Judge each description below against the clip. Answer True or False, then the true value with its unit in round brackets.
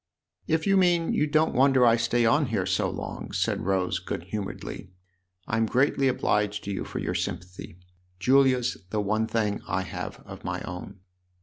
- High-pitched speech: False (110 Hz)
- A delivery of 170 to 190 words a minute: True (185 wpm)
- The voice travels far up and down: True (5.8 semitones)